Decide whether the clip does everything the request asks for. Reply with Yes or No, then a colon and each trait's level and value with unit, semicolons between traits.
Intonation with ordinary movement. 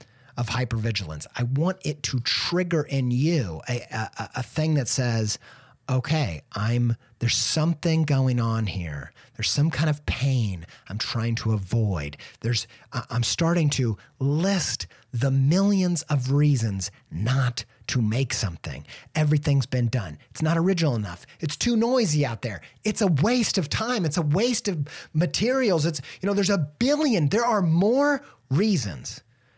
No: wide, 5.9 semitones